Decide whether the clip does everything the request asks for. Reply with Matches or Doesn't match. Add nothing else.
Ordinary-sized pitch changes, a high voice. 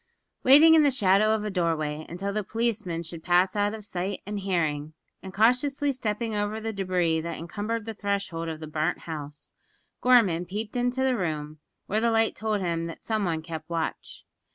Matches